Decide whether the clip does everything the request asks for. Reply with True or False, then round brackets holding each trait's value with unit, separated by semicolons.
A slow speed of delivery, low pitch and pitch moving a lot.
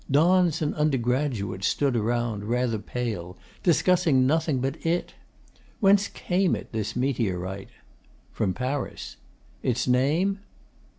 True (110 wpm; 130 Hz; 5.8 semitones)